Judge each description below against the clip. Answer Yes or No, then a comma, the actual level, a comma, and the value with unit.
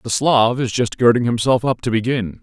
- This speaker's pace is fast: Yes, fast, 225 wpm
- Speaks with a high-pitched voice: No, low, 120 Hz